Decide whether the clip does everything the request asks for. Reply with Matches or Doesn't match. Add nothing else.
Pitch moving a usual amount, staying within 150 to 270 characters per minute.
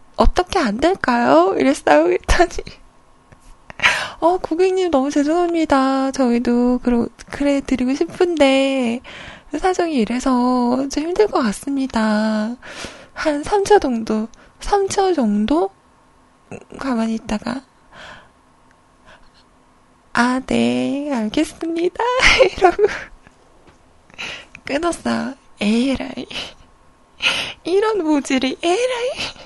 Doesn't match